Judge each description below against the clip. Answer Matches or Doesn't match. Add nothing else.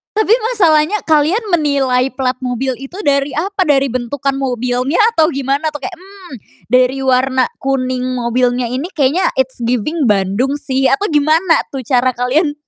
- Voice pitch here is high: Matches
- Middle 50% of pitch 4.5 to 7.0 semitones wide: Doesn't match